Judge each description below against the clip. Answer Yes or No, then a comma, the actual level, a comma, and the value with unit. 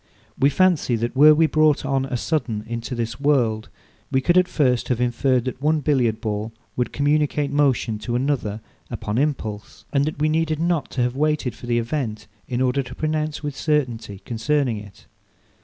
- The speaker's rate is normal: Yes, average, 185 wpm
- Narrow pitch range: No, average, 4.2 semitones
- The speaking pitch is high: No, low, 135 Hz